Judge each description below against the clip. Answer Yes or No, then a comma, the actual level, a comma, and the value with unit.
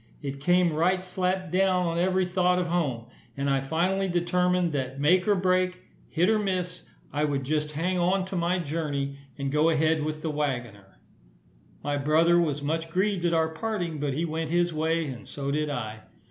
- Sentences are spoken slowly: No, average, 190 wpm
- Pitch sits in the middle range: Yes, medium, 165 Hz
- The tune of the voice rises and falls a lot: No, average, 3.7 semitones